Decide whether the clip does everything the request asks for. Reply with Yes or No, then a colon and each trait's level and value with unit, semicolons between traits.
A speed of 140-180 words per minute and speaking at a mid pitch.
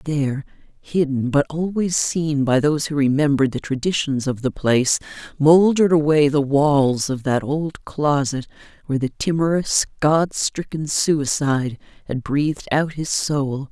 Yes: average, 145 wpm; medium, 145 Hz